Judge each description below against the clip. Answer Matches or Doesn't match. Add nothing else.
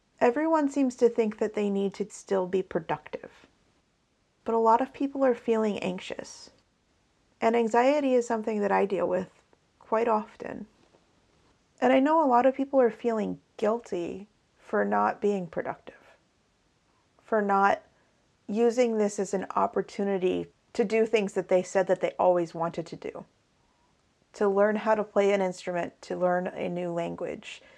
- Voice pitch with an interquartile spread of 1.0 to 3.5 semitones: Doesn't match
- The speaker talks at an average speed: Matches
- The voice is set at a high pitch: Matches